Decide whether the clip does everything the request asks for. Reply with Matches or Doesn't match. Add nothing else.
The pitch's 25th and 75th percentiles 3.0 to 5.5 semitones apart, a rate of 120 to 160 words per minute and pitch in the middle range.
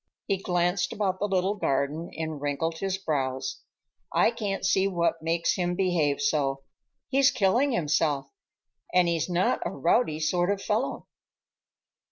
Matches